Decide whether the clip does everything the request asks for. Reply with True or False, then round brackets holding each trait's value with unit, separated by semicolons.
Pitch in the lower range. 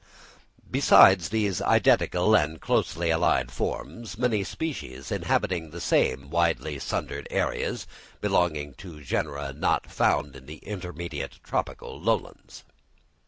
True (85 Hz)